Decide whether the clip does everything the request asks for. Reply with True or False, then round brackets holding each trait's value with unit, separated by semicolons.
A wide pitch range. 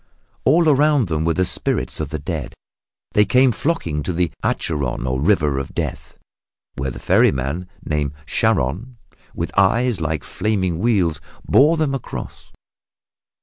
True (8.3 semitones)